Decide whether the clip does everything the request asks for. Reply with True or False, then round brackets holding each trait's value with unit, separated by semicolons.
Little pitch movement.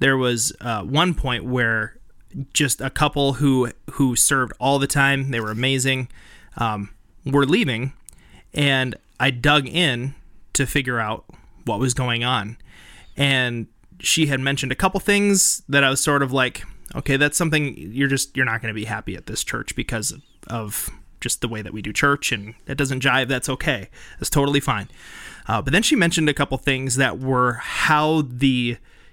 False (3.7 semitones)